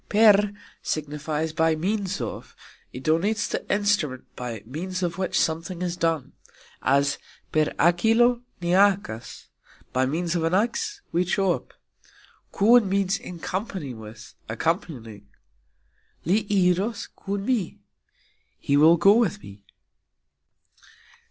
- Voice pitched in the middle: Yes, medium, 175 Hz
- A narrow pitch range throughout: No, average, 4.9 semitones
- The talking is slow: Yes, slow, 120 wpm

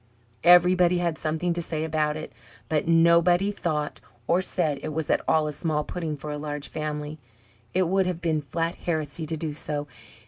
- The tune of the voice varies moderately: No, narrow, 2.3 semitones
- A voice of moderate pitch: Yes, medium, 160 Hz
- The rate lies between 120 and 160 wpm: No, average, 185 wpm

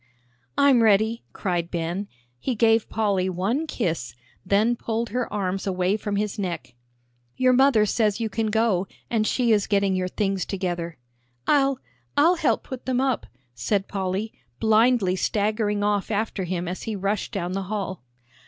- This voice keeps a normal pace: Yes, average, 160 wpm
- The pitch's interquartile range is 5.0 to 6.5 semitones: No, average, 3.4 semitones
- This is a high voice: Yes, high, 205 Hz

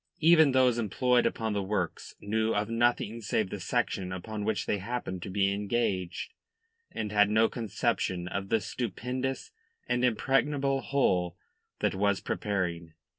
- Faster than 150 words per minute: No, average, 145 wpm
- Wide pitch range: No, average, 4.1 semitones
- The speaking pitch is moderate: No, low, 110 Hz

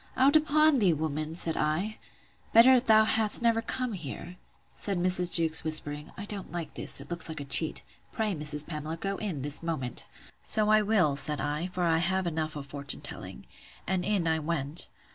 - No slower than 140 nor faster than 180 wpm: No, average, 190 wpm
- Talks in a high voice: No, medium, 170 Hz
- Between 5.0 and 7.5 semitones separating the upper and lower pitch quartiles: Yes, wide, 5.5 semitones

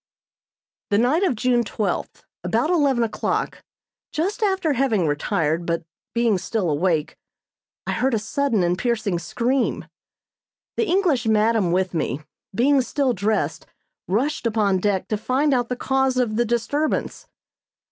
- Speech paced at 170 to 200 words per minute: No, average, 140 wpm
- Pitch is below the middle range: No, high, 235 Hz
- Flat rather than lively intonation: No, average, 5.2 semitones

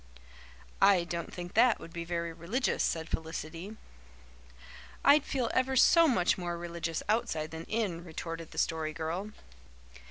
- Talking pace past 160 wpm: No, average, 140 wpm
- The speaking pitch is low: No, medium, 175 Hz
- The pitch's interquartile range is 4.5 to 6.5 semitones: Yes, average, 4.8 semitones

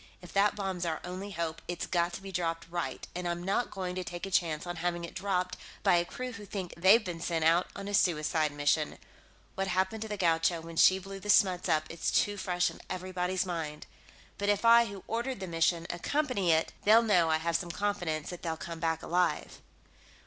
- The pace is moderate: No, fast, 220 wpm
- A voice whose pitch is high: No, medium, 180 Hz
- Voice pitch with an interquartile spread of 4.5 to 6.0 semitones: No, average, 2.8 semitones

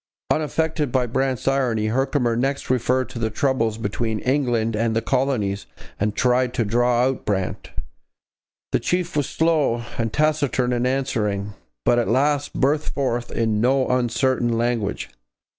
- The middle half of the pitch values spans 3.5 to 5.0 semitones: No, average, 3.0 semitones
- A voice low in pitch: Yes, low, 125 Hz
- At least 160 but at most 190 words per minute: No, average, 145 wpm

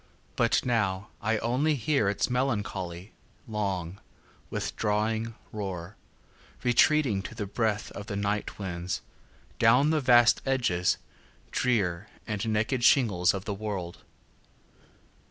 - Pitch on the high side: No, low, 105 Hz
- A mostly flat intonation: No, average, 3.6 semitones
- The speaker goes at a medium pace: No, slow, 100 wpm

